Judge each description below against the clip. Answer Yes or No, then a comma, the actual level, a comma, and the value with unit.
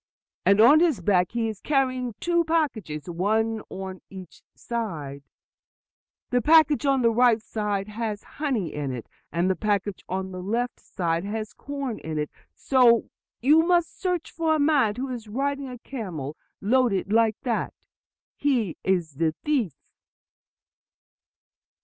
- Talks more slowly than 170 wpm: Yes, average, 145 wpm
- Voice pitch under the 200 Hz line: No, high, 225 Hz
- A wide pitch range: Yes, wide, 6.2 semitones